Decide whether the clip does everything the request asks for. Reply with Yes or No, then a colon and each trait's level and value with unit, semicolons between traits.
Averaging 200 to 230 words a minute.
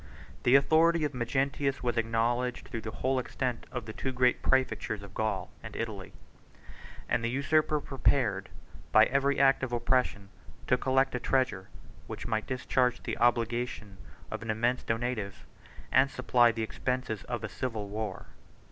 No: average, 155 wpm